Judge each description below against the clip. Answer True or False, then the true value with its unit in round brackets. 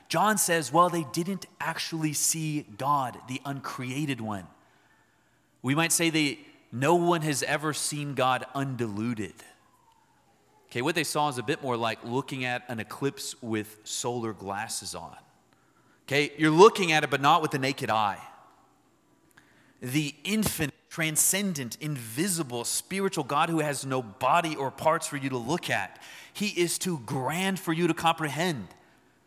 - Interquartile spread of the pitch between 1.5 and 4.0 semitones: False (4.4 semitones)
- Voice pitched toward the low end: False (150 Hz)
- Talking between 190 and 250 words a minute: False (155 wpm)